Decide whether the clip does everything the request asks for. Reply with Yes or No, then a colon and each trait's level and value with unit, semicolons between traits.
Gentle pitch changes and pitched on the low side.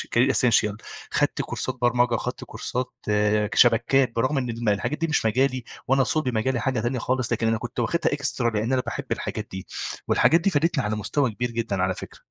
No: average, 3.1 semitones; low, 120 Hz